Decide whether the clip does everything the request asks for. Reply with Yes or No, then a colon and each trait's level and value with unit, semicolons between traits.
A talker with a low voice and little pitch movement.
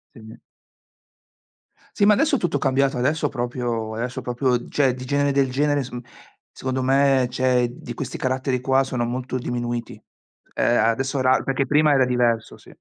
Yes: low, 130 Hz; narrow, 2.0 semitones